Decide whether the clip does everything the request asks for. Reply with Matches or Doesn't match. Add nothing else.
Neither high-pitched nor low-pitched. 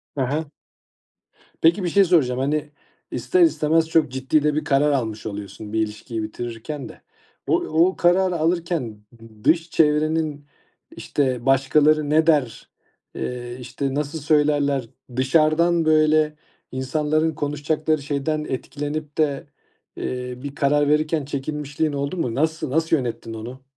Matches